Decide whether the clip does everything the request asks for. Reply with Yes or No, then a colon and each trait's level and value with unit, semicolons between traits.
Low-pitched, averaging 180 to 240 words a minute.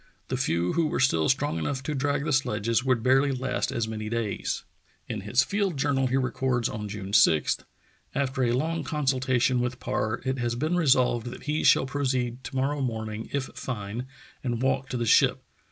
Yes: low, 130 Hz; average, 195 wpm